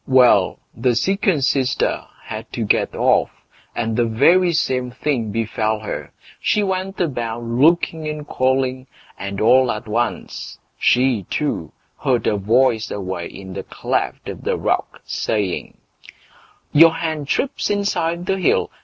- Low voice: Yes, low, 130 Hz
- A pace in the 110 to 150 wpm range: Yes, average, 140 wpm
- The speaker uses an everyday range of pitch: No, wide, 6.1 semitones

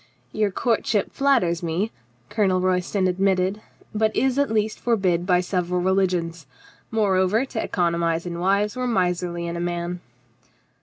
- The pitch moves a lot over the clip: No, average, 3.5 semitones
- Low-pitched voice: No, medium, 185 Hz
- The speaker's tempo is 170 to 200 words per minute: No, average, 145 wpm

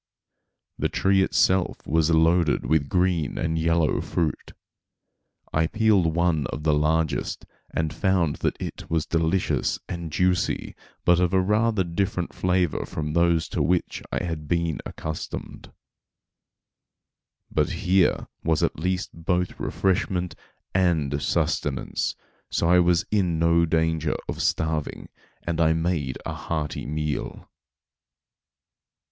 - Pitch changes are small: Yes, narrow, 2.2 semitones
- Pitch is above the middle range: No, very low, 85 Hz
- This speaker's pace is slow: Yes, slow, 125 wpm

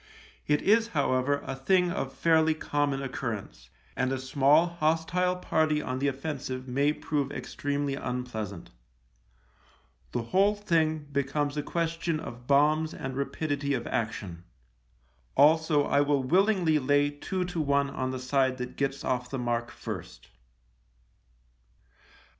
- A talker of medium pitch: Yes, medium, 145 Hz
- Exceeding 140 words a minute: No, slow, 135 wpm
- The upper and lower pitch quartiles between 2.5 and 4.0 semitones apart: Yes, average, 3.4 semitones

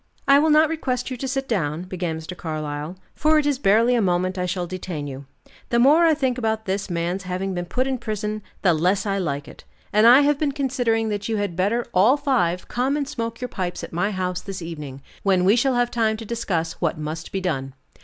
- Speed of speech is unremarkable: No, fast, 235 wpm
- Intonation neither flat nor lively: No, wide, 5.8 semitones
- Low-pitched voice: No, high, 200 Hz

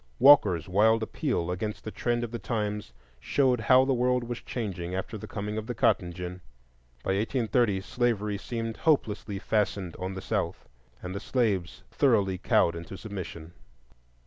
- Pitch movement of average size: Yes, average, 4.2 semitones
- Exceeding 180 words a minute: No, average, 160 wpm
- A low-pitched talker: Yes, low, 105 Hz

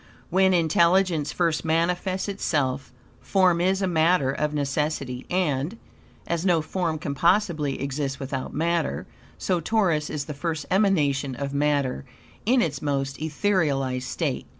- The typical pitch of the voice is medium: Yes, medium, 155 Hz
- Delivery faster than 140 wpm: No, slow, 135 wpm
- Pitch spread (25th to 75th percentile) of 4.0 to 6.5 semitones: Yes, average, 4.3 semitones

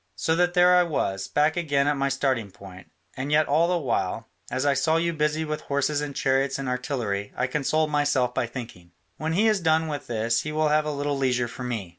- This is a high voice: No, medium, 140 Hz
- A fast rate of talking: Yes, fast, 230 wpm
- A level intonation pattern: No, average, 3.8 semitones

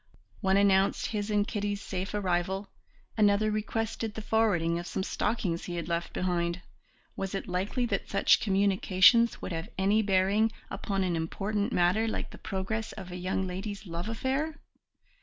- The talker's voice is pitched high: Yes, high, 195 Hz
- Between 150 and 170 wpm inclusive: Yes, average, 160 wpm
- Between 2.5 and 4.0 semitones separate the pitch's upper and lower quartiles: Yes, average, 2.9 semitones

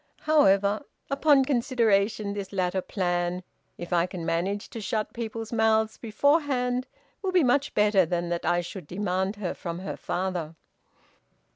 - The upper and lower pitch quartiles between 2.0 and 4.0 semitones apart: No, average, 4.7 semitones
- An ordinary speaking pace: Yes, average, 145 wpm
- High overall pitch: Yes, high, 205 Hz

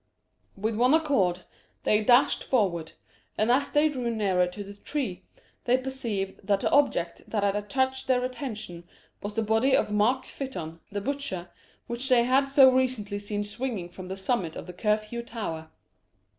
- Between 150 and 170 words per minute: Yes, average, 165 wpm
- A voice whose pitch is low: No, high, 220 Hz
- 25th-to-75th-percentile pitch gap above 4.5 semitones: Yes, average, 4.9 semitones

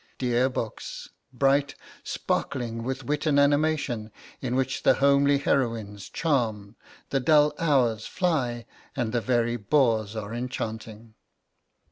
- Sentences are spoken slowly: Yes, slow, 120 wpm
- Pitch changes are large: No, average, 3.7 semitones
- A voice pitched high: No, low, 125 Hz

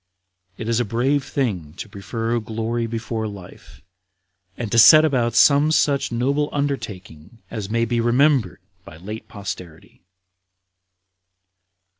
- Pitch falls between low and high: No, low, 115 Hz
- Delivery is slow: Yes, slow, 125 wpm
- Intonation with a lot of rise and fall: No, average, 4.1 semitones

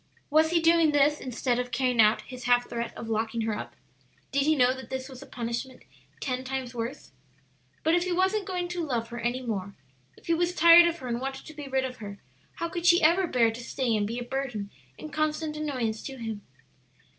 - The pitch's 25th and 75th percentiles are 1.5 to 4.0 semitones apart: No, average, 4.8 semitones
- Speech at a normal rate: No, fast, 225 wpm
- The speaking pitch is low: No, very high, 260 Hz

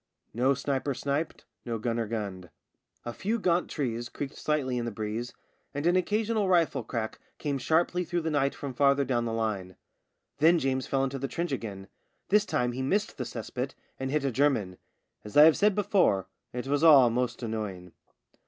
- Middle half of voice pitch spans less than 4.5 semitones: No, average, 5.2 semitones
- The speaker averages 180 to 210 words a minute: Yes, average, 190 wpm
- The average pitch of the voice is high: No, low, 135 Hz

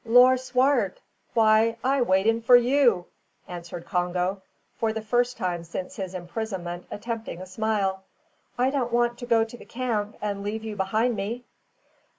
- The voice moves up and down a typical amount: Yes, average, 4.1 semitones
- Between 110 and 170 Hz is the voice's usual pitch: No, high, 220 Hz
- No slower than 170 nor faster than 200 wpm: No, average, 160 wpm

